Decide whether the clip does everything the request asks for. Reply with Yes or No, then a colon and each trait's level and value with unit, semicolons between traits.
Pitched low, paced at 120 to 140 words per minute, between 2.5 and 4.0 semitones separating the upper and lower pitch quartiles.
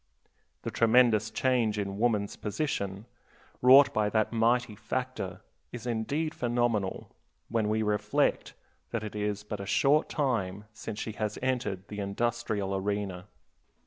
Yes: low, 110 Hz; slow, 135 wpm; average, 2.8 semitones